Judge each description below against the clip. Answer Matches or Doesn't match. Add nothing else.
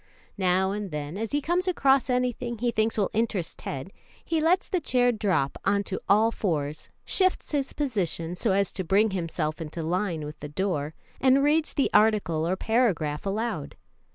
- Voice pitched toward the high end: Matches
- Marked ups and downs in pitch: Matches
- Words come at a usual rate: Matches